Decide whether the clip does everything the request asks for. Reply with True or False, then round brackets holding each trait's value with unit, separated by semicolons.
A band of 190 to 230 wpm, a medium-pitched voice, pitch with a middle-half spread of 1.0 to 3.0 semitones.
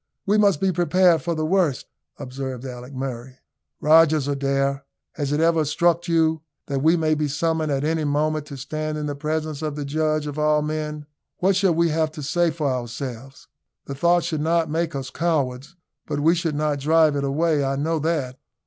True (195 wpm; 155 Hz; 2.7 semitones)